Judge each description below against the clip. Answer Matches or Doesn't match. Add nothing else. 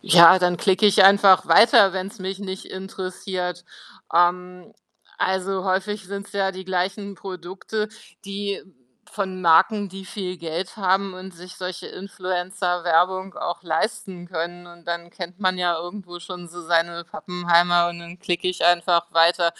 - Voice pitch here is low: Doesn't match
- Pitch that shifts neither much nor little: Doesn't match